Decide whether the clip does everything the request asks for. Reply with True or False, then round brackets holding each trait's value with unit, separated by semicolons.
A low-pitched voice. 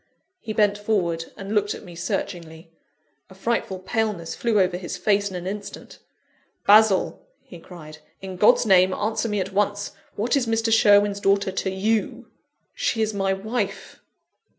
False (200 Hz)